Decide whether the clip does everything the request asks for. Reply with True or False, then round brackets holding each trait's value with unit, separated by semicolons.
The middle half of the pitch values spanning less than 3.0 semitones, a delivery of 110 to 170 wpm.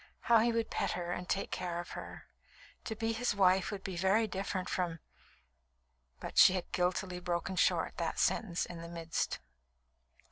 False (2.4 semitones; 180 wpm)